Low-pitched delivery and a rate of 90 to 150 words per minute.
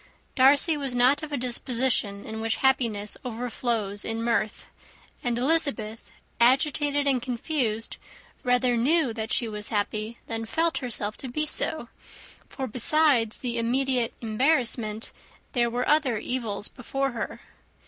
No: high, 245 Hz; slow, 135 wpm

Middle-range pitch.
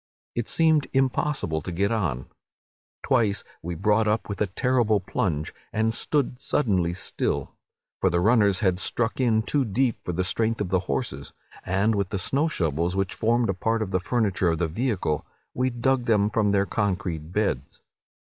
No: low, 105 Hz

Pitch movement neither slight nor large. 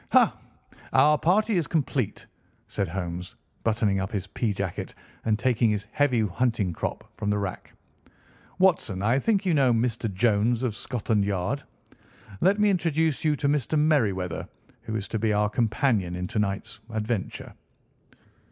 No: wide, 5.9 semitones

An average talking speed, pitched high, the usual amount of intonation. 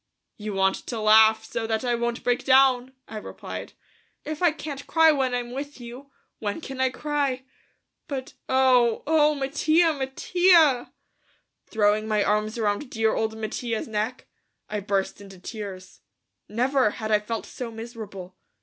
Yes: average, 150 wpm; high, 240 Hz; average, 3.9 semitones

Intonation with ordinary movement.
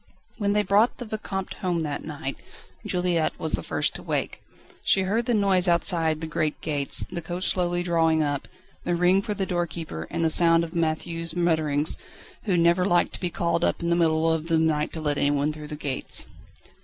No: narrow, 2.3 semitones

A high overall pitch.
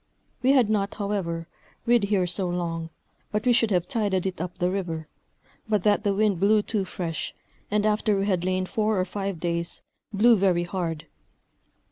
Yes: high, 195 Hz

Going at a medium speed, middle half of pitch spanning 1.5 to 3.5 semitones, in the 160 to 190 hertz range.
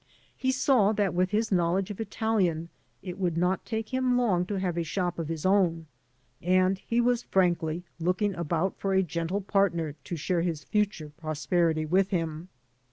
Yes: average, 175 wpm; average, 3.2 semitones; medium, 185 Hz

